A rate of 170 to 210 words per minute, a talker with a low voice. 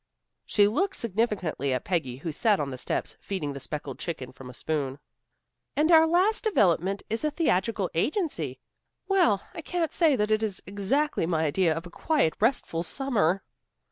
No: average, 175 wpm; high, 195 Hz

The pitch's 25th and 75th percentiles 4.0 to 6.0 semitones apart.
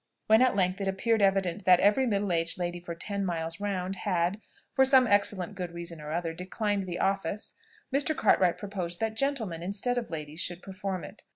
No: average, 3.0 semitones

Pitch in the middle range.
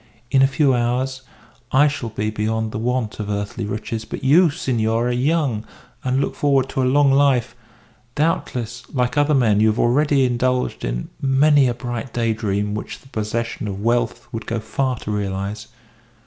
No: low, 120 Hz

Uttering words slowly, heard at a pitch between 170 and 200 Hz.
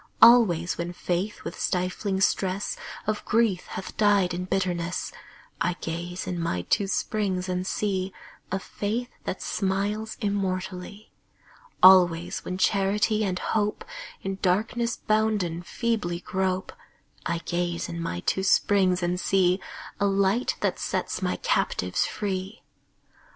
Yes: slow, 130 wpm; high, 190 Hz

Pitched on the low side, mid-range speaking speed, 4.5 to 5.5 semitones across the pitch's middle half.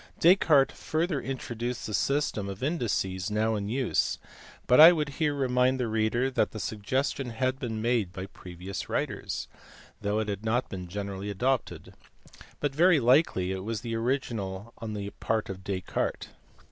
Yes: low, 115 Hz; average, 160 wpm; average, 4.8 semitones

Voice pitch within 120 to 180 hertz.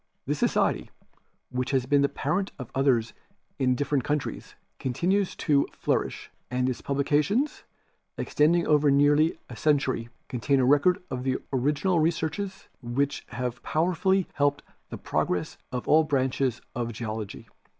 Yes: medium, 140 Hz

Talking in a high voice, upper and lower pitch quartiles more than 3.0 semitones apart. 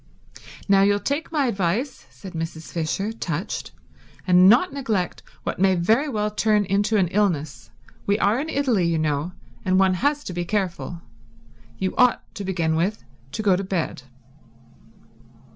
Yes: high, 195 Hz; average, 3.9 semitones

